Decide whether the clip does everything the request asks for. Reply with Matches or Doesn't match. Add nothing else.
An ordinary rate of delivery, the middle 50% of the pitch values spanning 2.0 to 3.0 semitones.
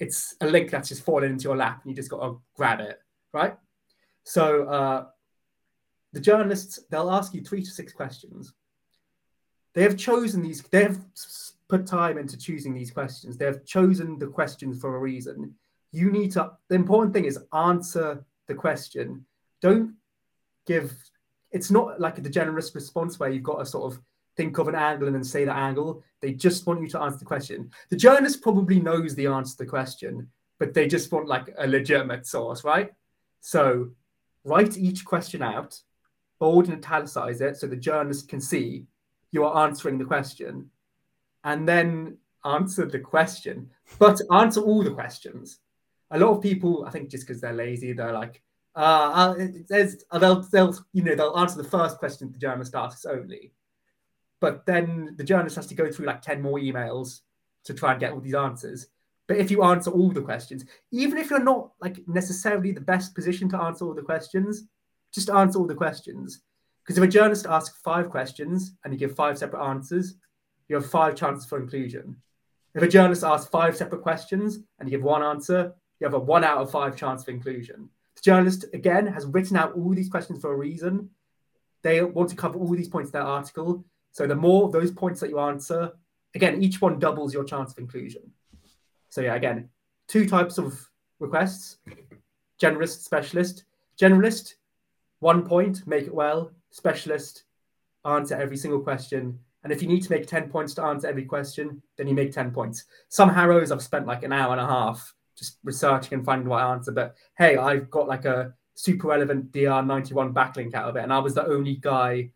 Doesn't match